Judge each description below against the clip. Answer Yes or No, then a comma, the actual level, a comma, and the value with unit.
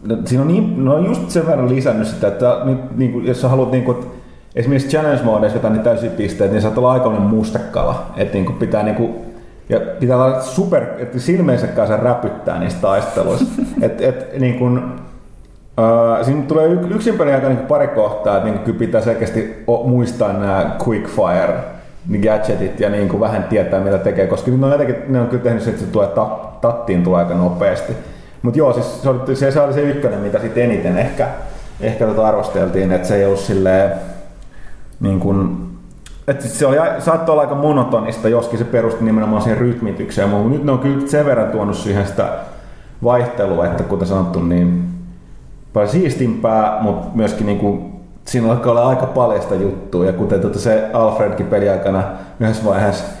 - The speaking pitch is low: Yes, low, 115 Hz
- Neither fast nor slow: No, fast, 180 wpm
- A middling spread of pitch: Yes, average, 4.1 semitones